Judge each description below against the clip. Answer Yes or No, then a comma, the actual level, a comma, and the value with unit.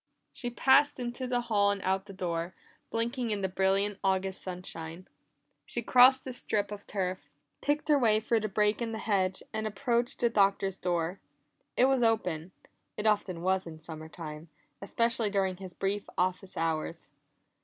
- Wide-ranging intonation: No, average, 4.0 semitones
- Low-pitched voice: No, high, 200 Hz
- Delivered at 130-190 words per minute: Yes, average, 170 wpm